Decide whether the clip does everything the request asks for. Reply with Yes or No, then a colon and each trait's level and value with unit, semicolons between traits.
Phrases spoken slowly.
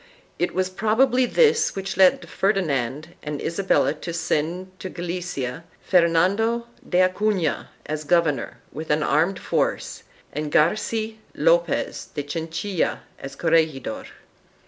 Yes: slow, 120 wpm